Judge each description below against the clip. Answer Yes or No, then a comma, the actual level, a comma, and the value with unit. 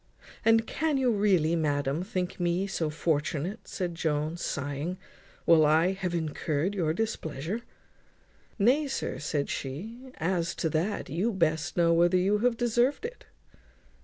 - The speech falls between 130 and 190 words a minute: Yes, average, 140 wpm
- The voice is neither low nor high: Yes, medium, 175 Hz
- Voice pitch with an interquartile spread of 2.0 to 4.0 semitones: No, average, 5.2 semitones